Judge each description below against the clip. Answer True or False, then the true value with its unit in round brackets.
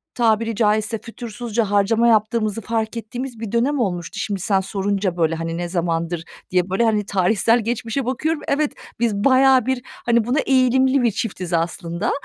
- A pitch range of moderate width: True (3.8 semitones)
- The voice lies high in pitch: True (220 Hz)